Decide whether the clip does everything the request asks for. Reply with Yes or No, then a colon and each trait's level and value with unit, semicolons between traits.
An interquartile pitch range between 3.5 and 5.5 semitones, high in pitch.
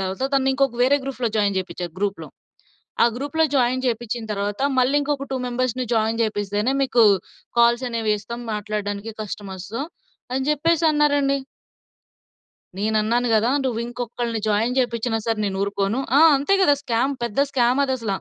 Yes: average, 3.8 semitones; high, 235 Hz